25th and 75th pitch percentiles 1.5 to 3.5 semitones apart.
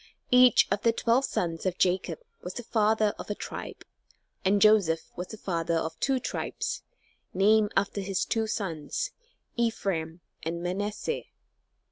No: average, 3.9 semitones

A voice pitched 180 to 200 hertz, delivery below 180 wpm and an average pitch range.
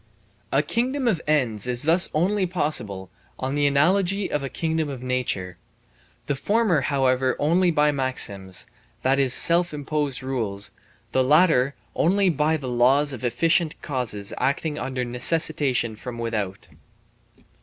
No: medium, 140 Hz; average, 140 wpm; average, 4.5 semitones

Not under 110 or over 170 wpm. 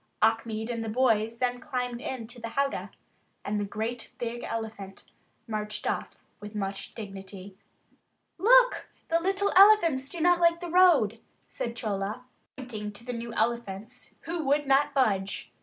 Yes: average, 150 wpm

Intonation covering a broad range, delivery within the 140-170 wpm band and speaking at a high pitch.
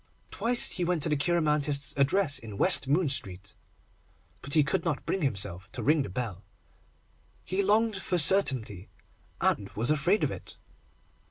No: wide, 6.3 semitones; average, 160 wpm; medium, 150 Hz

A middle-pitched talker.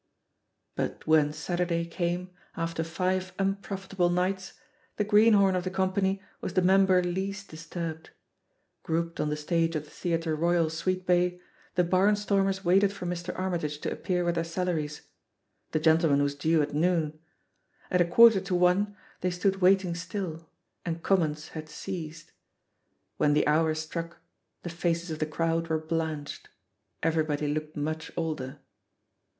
Yes: medium, 170 Hz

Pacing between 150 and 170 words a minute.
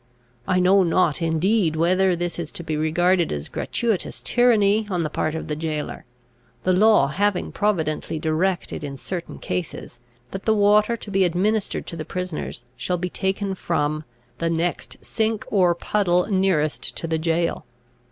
Yes: average, 160 wpm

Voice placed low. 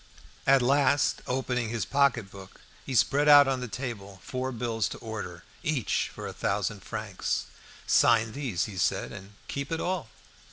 Yes: low, 125 Hz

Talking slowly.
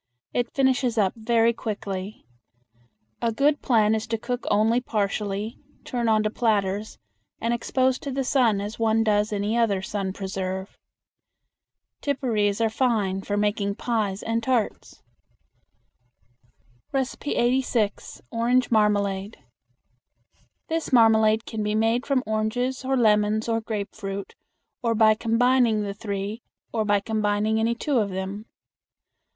Yes: slow, 125 wpm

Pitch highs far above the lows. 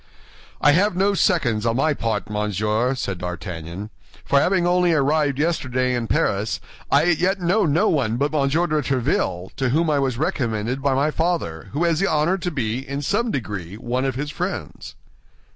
Yes: wide, 6.5 semitones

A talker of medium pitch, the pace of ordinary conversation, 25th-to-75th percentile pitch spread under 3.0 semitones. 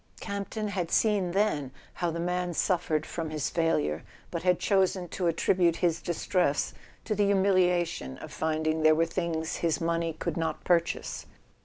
Yes: medium, 170 Hz; average, 165 wpm; narrow, 2.4 semitones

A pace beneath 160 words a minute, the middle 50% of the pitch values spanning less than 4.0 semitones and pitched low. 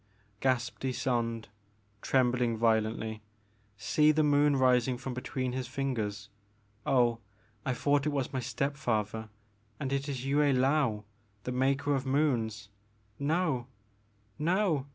Yes: slow, 135 wpm; average, 3.4 semitones; low, 130 Hz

